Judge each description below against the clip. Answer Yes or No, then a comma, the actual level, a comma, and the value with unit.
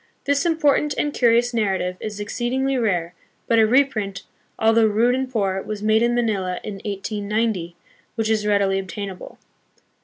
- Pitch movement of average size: Yes, average, 3.4 semitones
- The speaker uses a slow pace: No, average, 155 wpm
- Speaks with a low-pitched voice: No, high, 215 Hz